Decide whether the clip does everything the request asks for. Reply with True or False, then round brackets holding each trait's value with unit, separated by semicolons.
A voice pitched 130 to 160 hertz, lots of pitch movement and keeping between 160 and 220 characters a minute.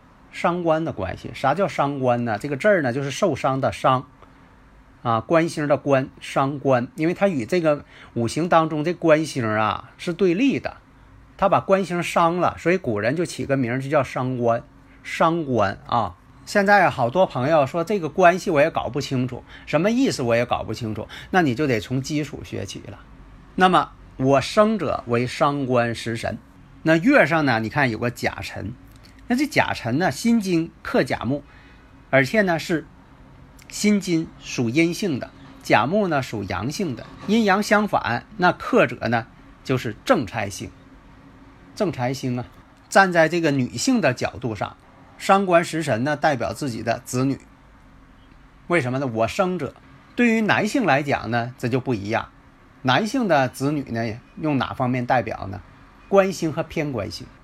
False (140 Hz; 5.7 semitones; 240 characters per minute)